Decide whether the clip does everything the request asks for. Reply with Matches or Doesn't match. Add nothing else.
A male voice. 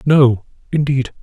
Matches